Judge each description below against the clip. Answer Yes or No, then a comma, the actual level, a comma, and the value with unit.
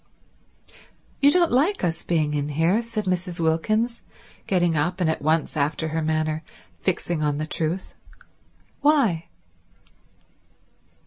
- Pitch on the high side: No, medium, 170 Hz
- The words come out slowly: Yes, slow, 125 wpm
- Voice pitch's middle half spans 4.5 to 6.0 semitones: Yes, average, 5.3 semitones